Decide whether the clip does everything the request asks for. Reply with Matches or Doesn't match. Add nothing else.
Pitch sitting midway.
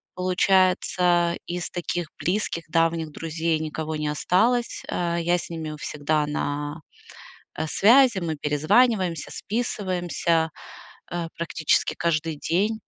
Matches